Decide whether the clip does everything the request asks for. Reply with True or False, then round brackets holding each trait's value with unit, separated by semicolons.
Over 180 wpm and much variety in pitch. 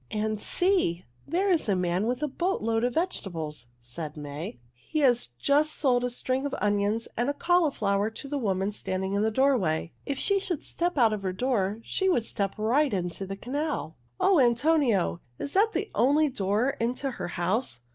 True (190 wpm; 6.8 semitones)